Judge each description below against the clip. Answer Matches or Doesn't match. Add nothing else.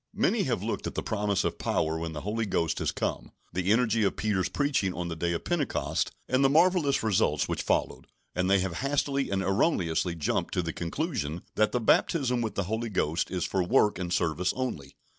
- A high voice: Doesn't match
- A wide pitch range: Matches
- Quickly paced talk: Matches